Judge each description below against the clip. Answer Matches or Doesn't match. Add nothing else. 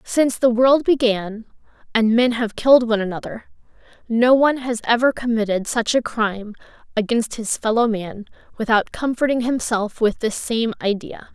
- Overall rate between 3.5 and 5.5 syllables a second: Matches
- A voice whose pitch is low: Doesn't match